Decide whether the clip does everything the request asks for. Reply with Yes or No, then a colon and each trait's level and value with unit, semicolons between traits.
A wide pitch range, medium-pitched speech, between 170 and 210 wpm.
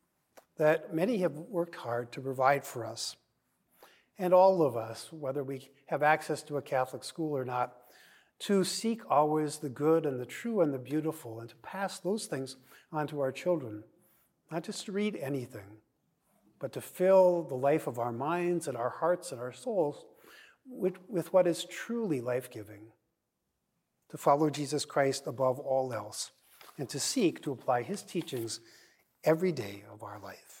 Yes: wide, 5.7 semitones; medium, 150 Hz; average, 175 wpm